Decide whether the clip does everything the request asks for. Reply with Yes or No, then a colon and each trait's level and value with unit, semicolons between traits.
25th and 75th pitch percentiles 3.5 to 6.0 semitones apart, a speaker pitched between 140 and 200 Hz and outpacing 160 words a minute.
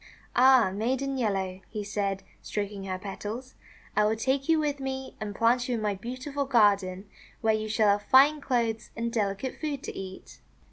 No: average, 4.4 semitones; high, 225 Hz; average, 180 wpm